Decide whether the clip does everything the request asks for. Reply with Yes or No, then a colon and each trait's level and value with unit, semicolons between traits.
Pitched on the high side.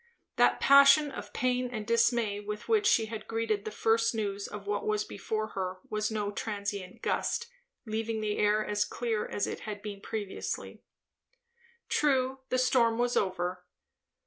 Yes: high, 215 Hz